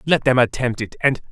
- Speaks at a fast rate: Yes, fast, 230 wpm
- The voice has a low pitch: Yes, low, 125 Hz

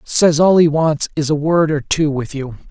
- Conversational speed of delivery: No, fast, 245 wpm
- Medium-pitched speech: Yes, medium, 155 Hz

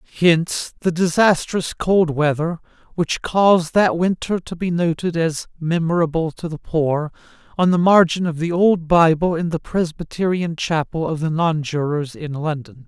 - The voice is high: No, medium, 165 Hz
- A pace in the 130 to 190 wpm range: Yes, average, 155 wpm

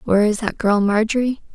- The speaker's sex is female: Yes, female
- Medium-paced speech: Yes, average, 195 wpm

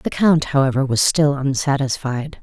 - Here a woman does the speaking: Yes, female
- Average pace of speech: Yes, average, 150 wpm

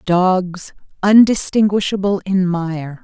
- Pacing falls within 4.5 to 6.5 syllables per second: No, 3.4 syllables/s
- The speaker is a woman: Yes, female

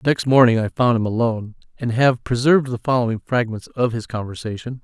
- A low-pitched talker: Yes, low, 120 Hz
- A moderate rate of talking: Yes, average, 185 wpm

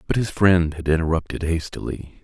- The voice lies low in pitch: Yes, very low, 85 Hz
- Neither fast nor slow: Yes, average, 160 wpm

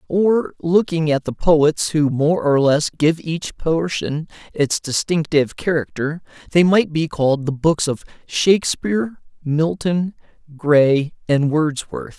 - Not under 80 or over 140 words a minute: Yes, slow, 135 wpm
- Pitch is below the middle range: No, medium, 160 Hz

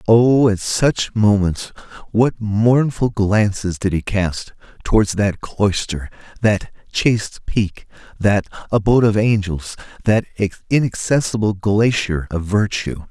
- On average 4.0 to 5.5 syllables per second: No, 3.8 syllables/s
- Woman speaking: No, male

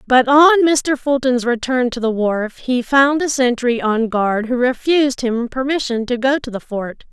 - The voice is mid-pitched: No, very high, 250 Hz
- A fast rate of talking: No, average, 195 wpm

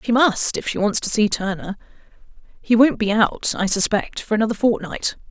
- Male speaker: No, female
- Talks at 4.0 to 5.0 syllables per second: No, 5.2 syllables/s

